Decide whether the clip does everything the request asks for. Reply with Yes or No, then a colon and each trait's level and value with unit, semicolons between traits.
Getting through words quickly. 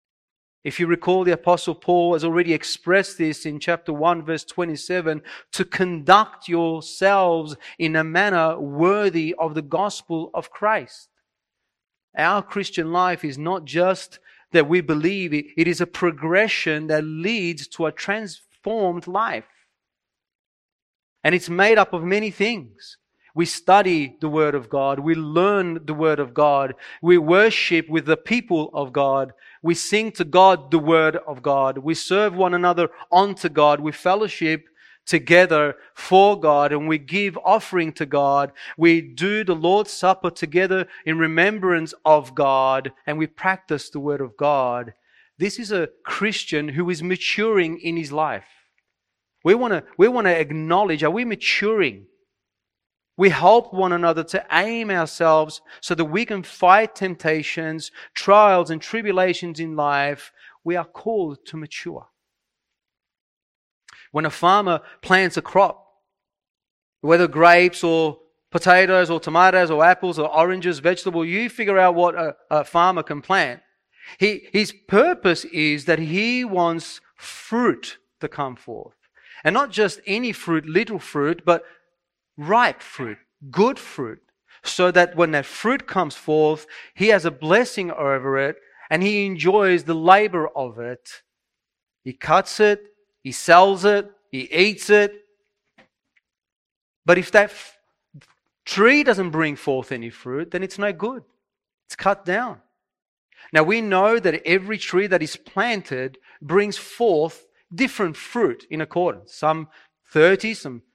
No: average, 145 wpm